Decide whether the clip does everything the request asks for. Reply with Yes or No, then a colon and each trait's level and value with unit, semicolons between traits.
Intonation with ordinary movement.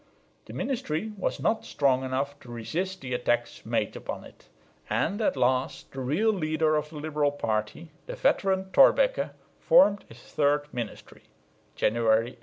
No: wide, 7.0 semitones